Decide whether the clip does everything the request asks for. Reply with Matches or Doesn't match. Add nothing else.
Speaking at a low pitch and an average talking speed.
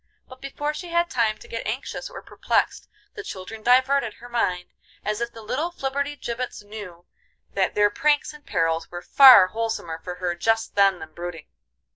Doesn't match